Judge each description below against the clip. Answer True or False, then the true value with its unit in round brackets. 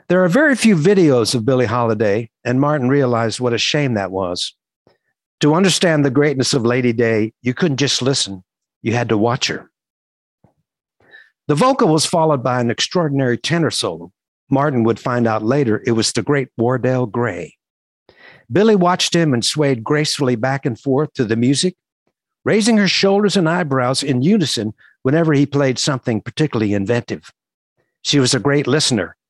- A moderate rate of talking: True (170 wpm)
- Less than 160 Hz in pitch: True (135 Hz)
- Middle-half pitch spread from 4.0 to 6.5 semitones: True (4.6 semitones)